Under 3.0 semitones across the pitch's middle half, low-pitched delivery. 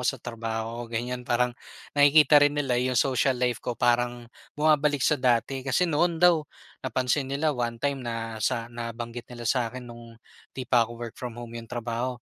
Yes: narrow, 2.6 semitones; low, 125 Hz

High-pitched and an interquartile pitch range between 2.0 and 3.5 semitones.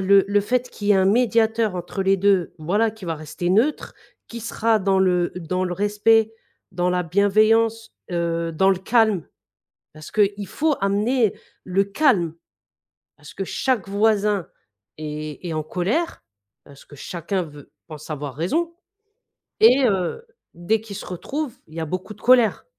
No: high, 195 Hz; average, 4.3 semitones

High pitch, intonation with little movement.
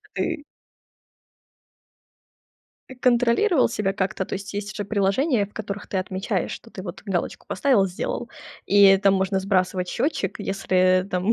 No: high, 200 Hz; average, 3.0 semitones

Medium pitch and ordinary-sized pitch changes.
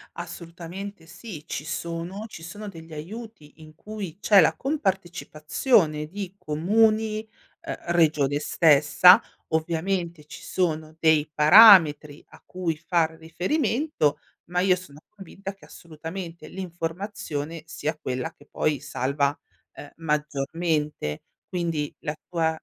Yes: medium, 165 Hz; average, 4.0 semitones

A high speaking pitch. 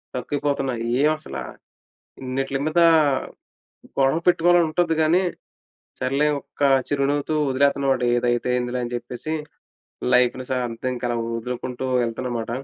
No: low, 130 Hz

